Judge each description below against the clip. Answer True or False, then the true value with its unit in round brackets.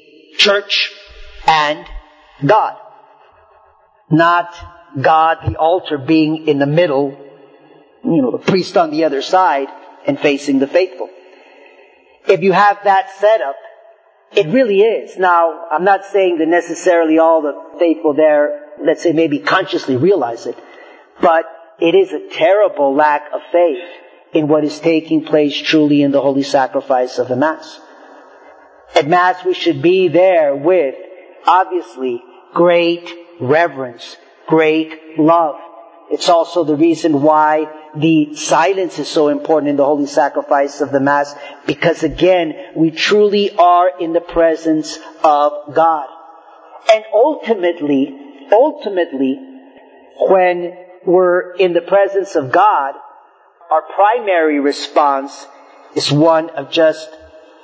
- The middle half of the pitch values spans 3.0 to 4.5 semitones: True (3.5 semitones)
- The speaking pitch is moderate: True (165 Hz)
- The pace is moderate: False (130 wpm)